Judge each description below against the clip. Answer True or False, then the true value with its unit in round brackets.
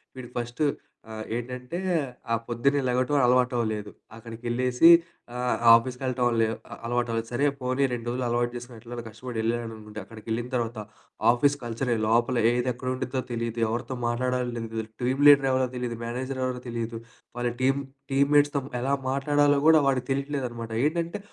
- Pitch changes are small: True (1.9 semitones)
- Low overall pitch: True (125 Hz)